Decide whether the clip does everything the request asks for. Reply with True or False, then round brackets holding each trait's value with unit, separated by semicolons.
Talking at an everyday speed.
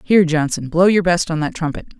False (240 wpm)